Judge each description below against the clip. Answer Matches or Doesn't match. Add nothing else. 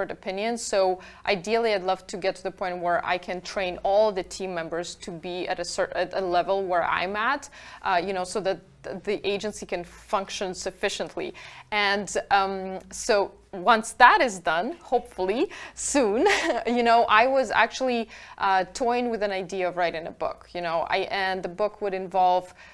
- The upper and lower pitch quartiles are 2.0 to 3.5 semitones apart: Matches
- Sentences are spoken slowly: Doesn't match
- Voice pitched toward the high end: Matches